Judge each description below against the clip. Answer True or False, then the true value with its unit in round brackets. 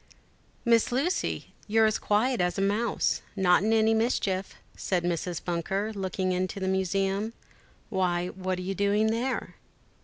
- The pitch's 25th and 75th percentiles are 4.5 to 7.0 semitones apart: False (3.0 semitones)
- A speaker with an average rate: True (150 wpm)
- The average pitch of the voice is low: False (195 Hz)